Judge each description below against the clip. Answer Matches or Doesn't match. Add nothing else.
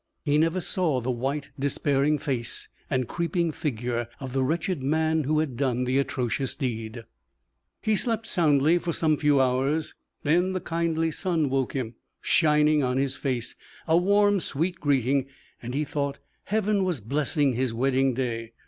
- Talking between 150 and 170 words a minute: Matches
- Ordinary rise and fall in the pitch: Matches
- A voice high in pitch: Doesn't match